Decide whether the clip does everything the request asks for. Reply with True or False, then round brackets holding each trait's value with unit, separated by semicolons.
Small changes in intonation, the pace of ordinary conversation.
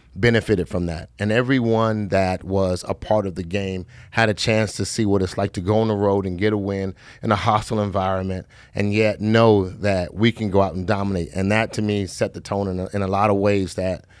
False (2.3 semitones; 245 wpm)